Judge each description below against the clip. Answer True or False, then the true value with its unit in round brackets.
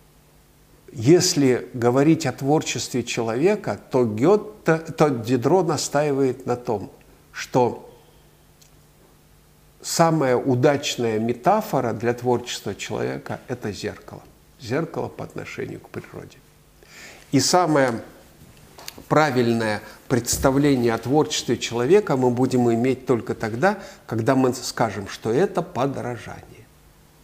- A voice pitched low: True (130 Hz)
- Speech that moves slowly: True (95 wpm)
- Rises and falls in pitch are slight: False (4.0 semitones)